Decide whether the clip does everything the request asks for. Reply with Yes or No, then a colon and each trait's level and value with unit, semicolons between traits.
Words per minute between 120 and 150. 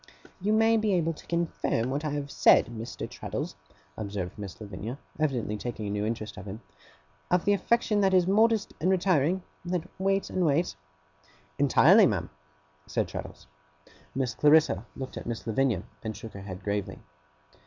No: average, 165 wpm